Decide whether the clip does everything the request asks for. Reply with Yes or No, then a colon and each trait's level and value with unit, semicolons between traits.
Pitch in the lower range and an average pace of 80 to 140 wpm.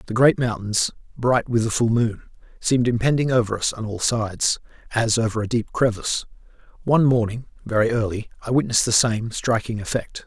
No: low, 115 Hz; average, 175 wpm